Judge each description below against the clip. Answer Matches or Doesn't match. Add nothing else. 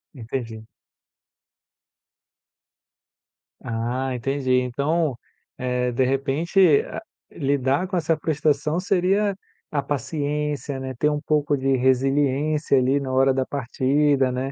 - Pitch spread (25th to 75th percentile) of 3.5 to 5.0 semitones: Doesn't match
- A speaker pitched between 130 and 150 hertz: Matches